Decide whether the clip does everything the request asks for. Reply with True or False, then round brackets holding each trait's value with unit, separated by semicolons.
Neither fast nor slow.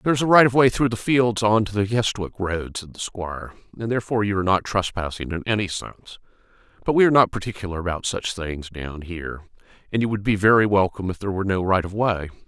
False (235 wpm)